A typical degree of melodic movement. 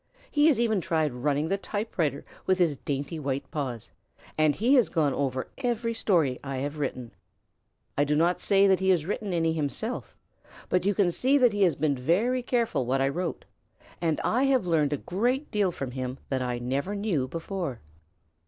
No: wide, 6.6 semitones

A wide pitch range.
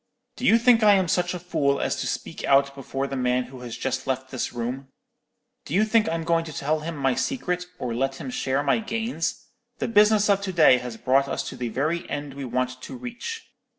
Yes: wide, 7.3 semitones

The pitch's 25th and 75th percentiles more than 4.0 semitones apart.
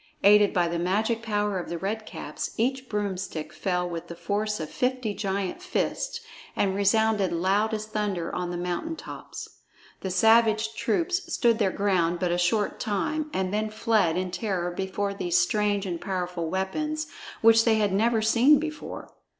No: average, 3.4 semitones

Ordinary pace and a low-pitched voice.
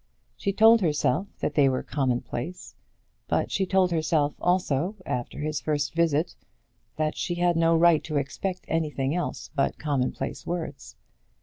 No: average, 145 wpm; medium, 155 Hz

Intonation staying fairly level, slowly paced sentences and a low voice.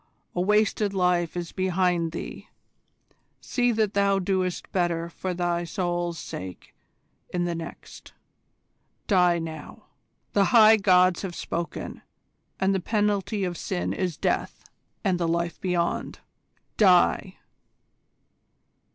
No: narrow, 2.3 semitones; slow, 115 wpm; medium, 180 Hz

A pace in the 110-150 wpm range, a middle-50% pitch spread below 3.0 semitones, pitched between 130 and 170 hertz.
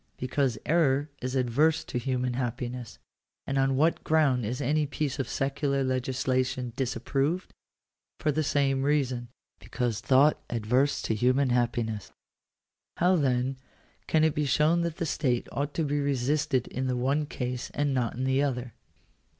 No: average, 160 wpm; narrow, 2.6 semitones; low, 135 Hz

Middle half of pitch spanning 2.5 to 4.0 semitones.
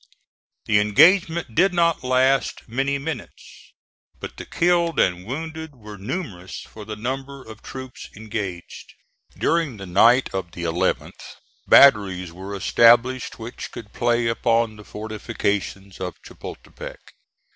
No: average, 5.2 semitones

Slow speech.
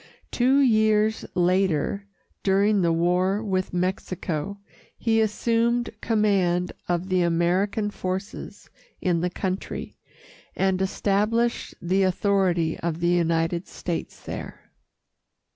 Yes: slow, 105 wpm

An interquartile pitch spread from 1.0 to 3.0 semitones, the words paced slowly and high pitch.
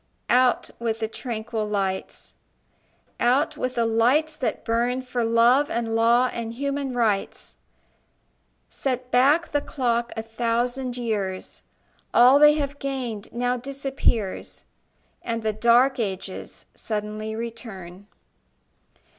Yes: narrow, 2.5 semitones; slow, 115 wpm; high, 235 Hz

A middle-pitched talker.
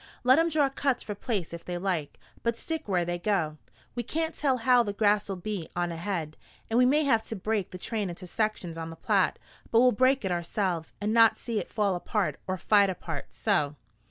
No: high, 205 Hz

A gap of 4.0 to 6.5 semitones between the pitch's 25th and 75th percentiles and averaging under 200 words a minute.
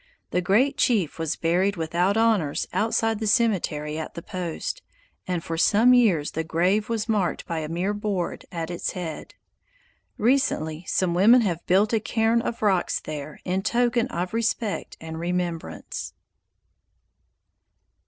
Yes: average, 5.1 semitones; average, 145 wpm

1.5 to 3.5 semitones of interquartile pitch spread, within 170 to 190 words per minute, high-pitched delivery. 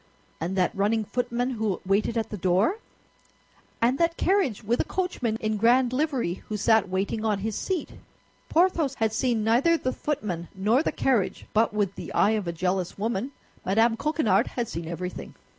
No: average, 4.5 semitones; average, 175 wpm; high, 220 Hz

